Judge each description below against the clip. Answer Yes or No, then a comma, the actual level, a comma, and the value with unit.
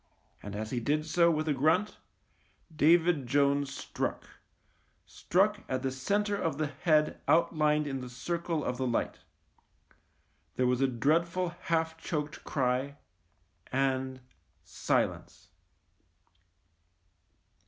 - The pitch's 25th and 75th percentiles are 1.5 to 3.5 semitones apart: No, average, 4.1 semitones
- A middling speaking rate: No, slow, 120 wpm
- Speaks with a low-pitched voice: No, medium, 150 Hz